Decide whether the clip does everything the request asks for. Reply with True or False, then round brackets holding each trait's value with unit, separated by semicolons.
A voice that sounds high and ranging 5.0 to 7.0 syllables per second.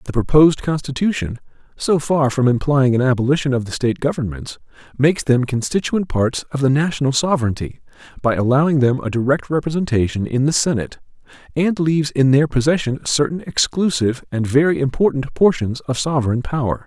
False (135 Hz; 5.9 syllables/s)